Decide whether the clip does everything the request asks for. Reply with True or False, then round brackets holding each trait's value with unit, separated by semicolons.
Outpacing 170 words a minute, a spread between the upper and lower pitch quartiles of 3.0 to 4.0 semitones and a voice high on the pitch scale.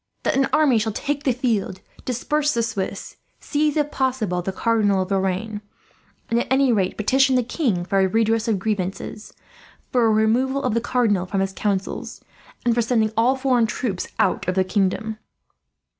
False (180 wpm; 4.6 semitones; 225 Hz)